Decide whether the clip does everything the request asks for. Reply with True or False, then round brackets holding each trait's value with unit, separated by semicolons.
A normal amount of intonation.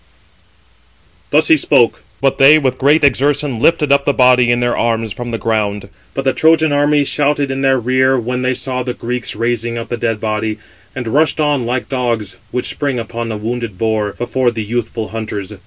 True (3.2 semitones)